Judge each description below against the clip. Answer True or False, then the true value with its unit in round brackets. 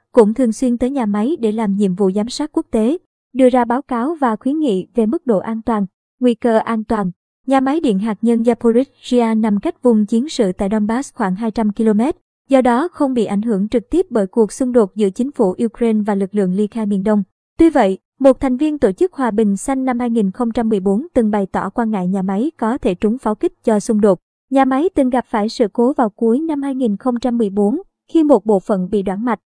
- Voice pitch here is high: True (230 Hz)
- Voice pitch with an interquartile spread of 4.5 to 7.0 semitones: False (3.5 semitones)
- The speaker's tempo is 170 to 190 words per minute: False (230 wpm)